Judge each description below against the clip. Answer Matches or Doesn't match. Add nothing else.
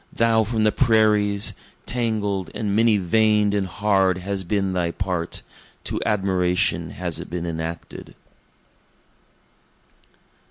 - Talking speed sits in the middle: Doesn't match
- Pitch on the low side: Matches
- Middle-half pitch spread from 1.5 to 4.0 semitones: Matches